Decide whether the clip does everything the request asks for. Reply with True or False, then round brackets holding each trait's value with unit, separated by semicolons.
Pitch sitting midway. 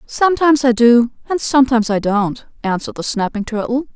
False (240 Hz)